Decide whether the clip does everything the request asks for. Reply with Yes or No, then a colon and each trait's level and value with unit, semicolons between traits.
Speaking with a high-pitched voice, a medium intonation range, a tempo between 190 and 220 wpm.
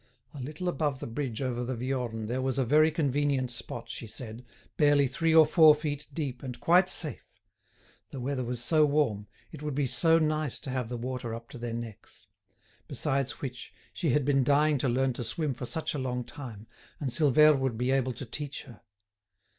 No: low, 135 Hz; average, 3.4 semitones; average, 200 wpm